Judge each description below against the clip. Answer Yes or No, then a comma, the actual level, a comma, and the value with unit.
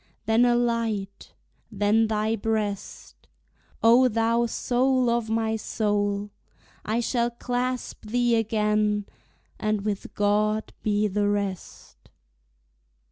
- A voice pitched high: Yes, high, 220 Hz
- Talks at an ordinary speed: No, slow, 105 wpm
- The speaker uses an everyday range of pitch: No, narrow, 2.2 semitones